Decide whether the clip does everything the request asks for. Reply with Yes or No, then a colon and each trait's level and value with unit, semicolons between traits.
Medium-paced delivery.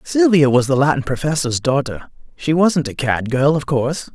Yes: average, 190 wpm